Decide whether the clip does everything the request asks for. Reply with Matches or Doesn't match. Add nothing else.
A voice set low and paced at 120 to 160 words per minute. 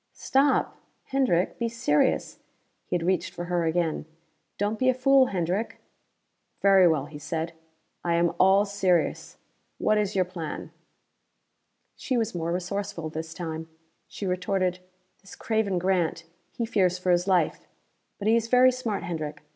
Doesn't match